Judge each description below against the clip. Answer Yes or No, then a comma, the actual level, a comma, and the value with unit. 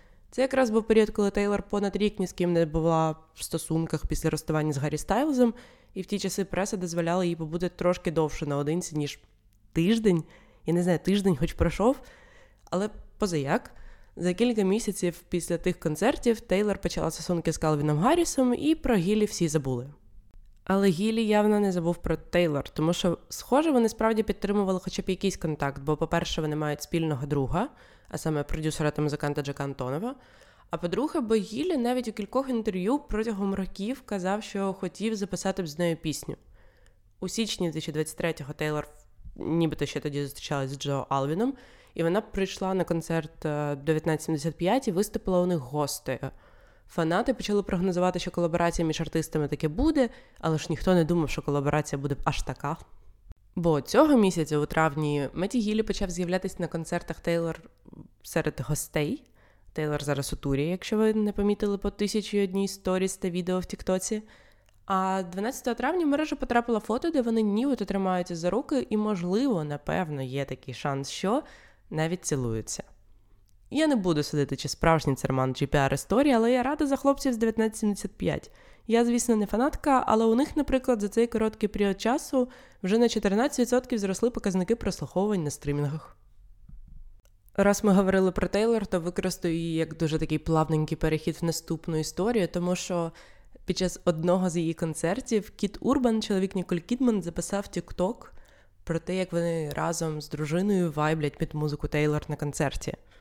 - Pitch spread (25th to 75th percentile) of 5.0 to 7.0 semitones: Yes, wide, 5.5 semitones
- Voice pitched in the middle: Yes, medium, 180 Hz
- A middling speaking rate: No, fast, 165 wpm